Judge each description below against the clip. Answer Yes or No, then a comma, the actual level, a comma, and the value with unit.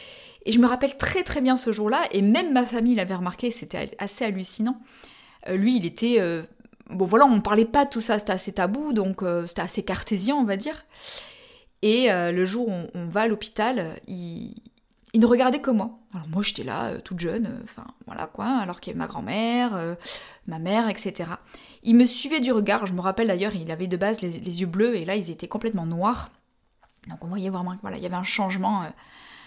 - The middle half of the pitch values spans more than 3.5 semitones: Yes, average, 4.2 semitones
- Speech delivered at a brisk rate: Yes, fast, 230 wpm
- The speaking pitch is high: Yes, high, 215 Hz